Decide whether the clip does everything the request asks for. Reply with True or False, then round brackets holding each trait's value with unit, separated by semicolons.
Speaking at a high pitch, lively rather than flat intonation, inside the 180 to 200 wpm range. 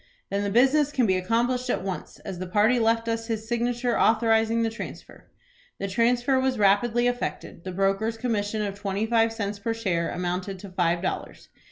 False (225 Hz; 3.3 semitones; 185 wpm)